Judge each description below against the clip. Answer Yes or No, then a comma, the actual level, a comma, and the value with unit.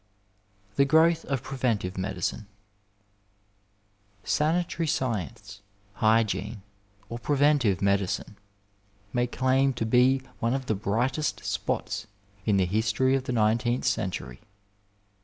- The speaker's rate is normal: No, slow, 105 wpm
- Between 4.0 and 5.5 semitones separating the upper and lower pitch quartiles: Yes, average, 4.5 semitones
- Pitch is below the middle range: Yes, low, 120 Hz